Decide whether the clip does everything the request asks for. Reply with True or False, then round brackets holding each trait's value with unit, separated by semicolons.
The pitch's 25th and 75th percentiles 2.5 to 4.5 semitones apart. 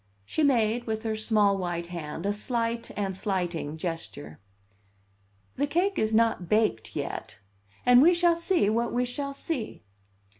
False (5.2 semitones)